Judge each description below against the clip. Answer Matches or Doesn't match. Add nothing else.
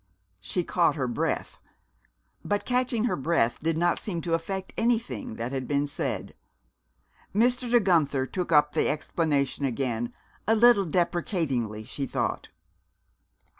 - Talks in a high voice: Doesn't match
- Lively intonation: Matches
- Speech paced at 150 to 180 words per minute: Doesn't match